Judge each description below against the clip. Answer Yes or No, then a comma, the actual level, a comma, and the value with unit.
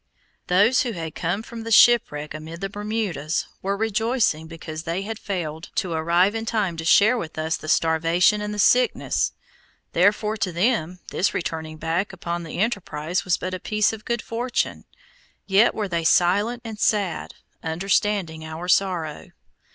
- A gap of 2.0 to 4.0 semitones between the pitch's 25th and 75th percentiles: No, average, 4.6 semitones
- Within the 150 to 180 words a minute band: Yes, average, 165 wpm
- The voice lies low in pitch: No, medium, 185 Hz